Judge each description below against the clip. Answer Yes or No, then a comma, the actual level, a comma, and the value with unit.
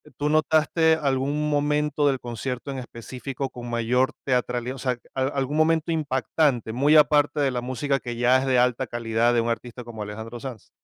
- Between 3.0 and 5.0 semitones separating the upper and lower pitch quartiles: Yes, average, 3.3 semitones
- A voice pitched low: Yes, low, 130 Hz